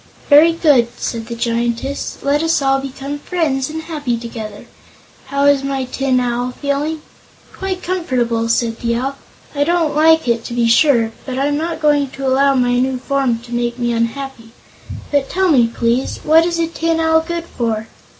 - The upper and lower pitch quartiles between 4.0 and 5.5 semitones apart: Yes, average, 4.4 semitones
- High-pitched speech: Yes, very high, 270 Hz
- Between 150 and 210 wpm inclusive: Yes, average, 185 wpm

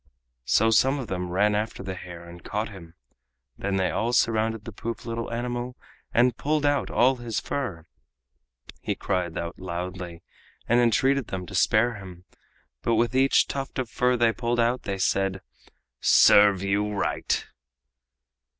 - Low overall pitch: Yes, low, 110 Hz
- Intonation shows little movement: No, average, 4.4 semitones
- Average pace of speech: Yes, average, 160 wpm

